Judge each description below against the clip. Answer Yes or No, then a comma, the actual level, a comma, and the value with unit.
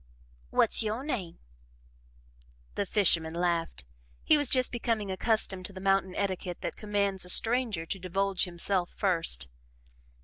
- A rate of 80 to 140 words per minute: Yes, slow, 135 wpm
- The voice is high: Yes, high, 195 Hz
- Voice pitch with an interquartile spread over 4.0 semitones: No, average, 3.2 semitones